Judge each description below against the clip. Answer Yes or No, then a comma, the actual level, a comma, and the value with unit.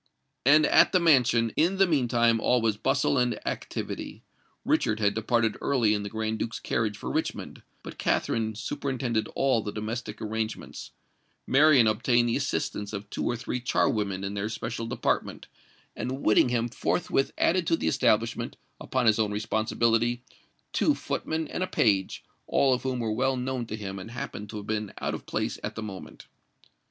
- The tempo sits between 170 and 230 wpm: Yes, average, 175 wpm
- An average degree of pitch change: Yes, average, 3.1 semitones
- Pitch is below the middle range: Yes, low, 115 Hz